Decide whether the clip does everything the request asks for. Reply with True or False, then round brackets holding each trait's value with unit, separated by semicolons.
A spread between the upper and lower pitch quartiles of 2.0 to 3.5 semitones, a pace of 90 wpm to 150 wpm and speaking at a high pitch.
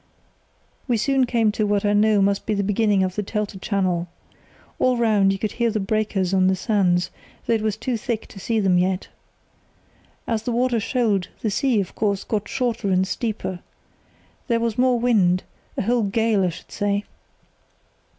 False (2.9 semitones; 180 wpm; 210 Hz)